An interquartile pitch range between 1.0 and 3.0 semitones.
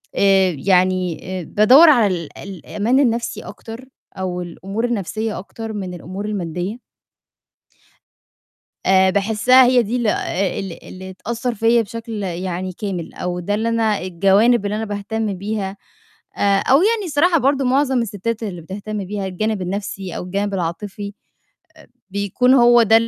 No: average, 3.6 semitones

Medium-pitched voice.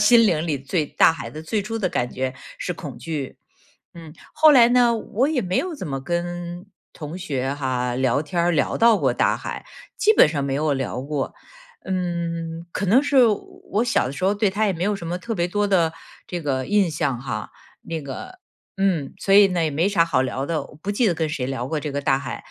Yes: medium, 170 Hz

